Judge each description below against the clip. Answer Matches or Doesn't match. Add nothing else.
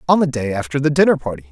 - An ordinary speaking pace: Doesn't match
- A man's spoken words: Matches